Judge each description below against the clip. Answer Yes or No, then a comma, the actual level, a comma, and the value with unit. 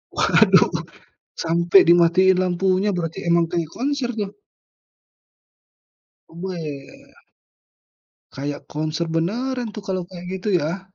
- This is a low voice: No, medium, 180 Hz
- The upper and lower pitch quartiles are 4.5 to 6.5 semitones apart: No, average, 2.8 semitones